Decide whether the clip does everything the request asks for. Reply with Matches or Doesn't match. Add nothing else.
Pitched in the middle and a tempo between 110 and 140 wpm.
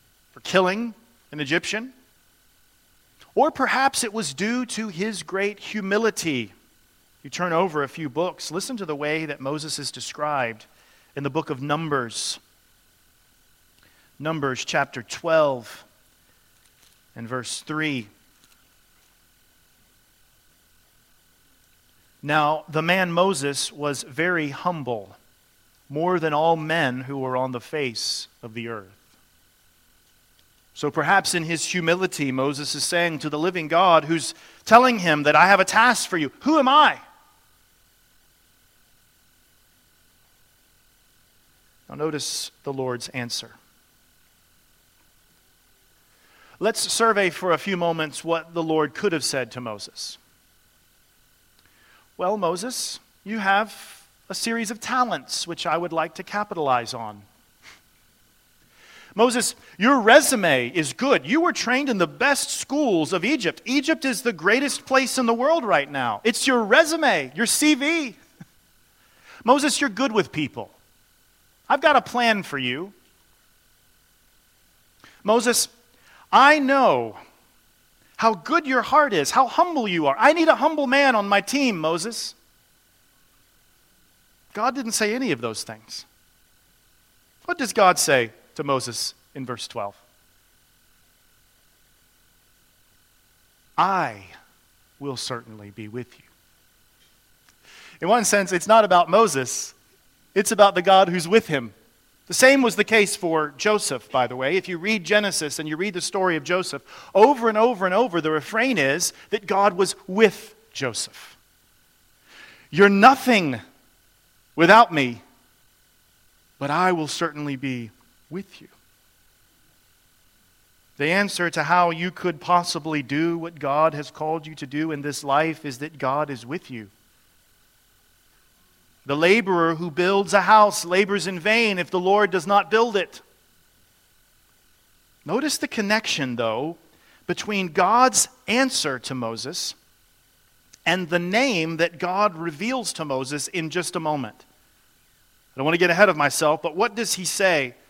Matches